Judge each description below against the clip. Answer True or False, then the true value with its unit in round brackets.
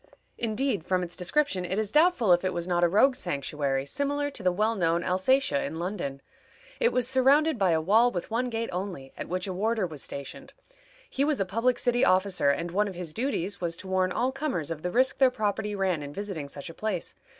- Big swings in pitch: True (5.9 semitones)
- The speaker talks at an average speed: False (225 wpm)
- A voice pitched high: True (195 Hz)